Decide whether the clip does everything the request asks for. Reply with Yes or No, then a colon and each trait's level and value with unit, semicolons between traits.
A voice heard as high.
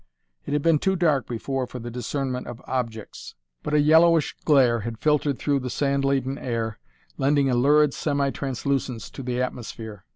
No: low, 135 Hz